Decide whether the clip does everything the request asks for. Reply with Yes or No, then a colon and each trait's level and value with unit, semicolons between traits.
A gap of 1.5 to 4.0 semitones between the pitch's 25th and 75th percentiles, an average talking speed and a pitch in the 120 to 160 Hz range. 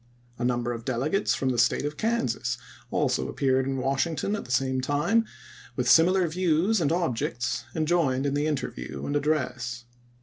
No: average, 4.6 semitones; average, 175 wpm; medium, 140 Hz